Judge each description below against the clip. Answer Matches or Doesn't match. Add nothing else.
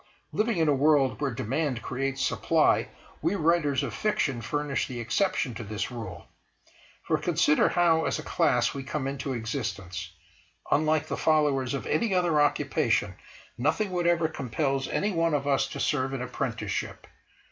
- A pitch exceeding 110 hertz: Matches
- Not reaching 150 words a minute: Doesn't match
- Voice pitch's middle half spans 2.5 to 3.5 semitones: Doesn't match